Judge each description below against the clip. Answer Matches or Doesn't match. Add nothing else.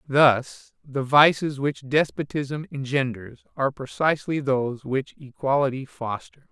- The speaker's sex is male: Matches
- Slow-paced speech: Matches